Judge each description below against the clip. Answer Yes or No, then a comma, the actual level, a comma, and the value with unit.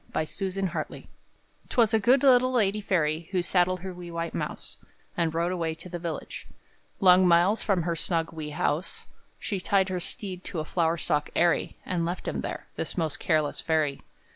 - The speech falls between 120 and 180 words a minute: No, average, 190 wpm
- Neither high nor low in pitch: Yes, medium, 175 Hz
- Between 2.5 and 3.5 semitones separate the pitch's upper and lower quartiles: Yes, average, 2.8 semitones